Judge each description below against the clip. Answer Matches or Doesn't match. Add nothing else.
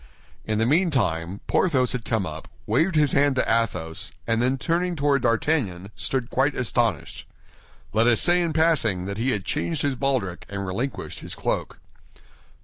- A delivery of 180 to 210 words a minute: Doesn't match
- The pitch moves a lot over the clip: Matches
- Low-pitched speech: Matches